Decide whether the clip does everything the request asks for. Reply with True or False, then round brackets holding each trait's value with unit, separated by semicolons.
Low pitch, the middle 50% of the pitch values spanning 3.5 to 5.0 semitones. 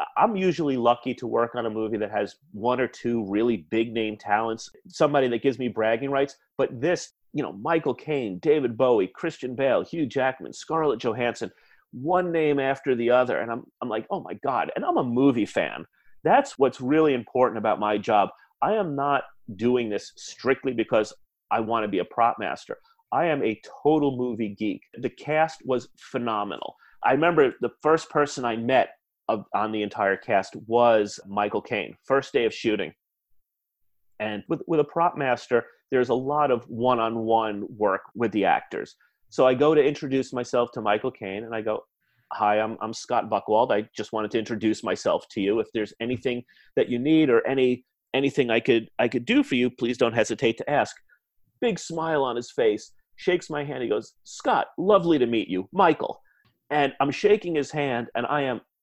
True (125 Hz; 4.5 semitones)